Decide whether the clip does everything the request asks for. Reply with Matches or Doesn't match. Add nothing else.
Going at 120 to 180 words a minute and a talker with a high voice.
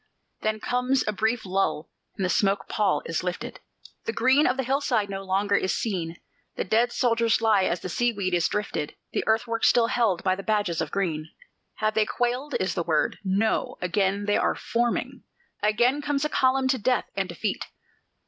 Doesn't match